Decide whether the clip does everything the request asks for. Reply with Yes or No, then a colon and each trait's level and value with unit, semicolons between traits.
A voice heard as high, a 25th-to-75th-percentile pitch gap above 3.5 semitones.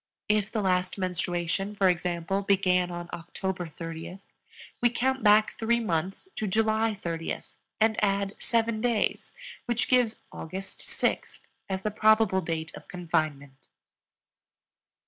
Yes: high, 195 Hz; average, 3.9 semitones